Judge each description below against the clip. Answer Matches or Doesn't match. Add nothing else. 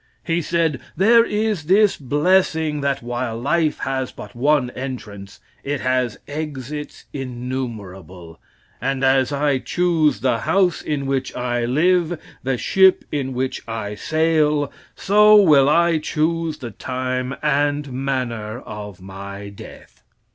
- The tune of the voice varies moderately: Matches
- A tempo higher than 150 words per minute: Doesn't match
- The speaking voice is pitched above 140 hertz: Doesn't match